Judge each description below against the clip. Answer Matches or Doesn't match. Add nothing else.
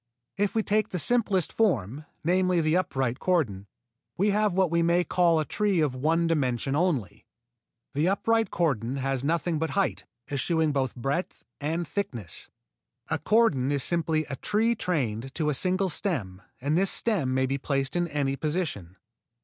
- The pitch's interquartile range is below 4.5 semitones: Doesn't match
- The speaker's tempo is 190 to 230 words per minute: Doesn't match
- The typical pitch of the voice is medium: Matches